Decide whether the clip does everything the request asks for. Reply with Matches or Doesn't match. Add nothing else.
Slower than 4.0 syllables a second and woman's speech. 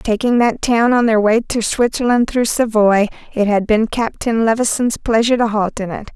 Doesn't match